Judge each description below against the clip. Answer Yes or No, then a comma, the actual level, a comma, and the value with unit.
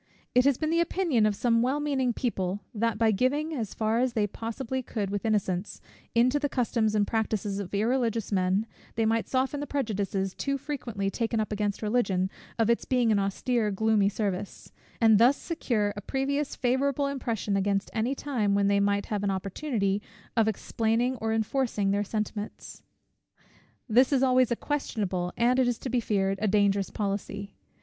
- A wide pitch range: No, average, 4.0 semitones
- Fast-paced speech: No, average, 180 wpm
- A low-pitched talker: No, high, 225 Hz